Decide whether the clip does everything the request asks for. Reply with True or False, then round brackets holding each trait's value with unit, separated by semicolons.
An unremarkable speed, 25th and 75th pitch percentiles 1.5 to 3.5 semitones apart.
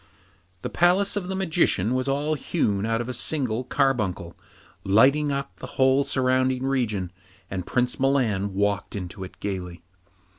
False (150 wpm; 5.5 semitones)